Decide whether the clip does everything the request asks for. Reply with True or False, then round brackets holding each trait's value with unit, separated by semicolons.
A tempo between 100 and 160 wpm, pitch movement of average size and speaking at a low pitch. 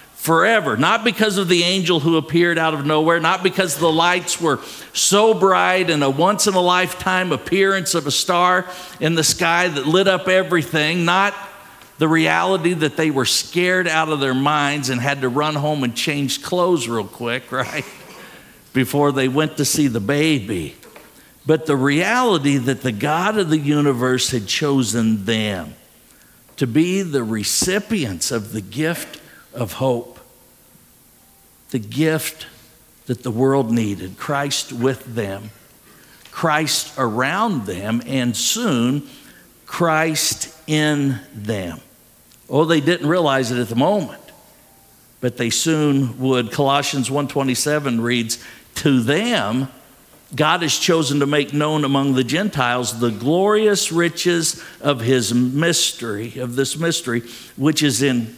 False (145 wpm; 5.0 semitones; 145 Hz)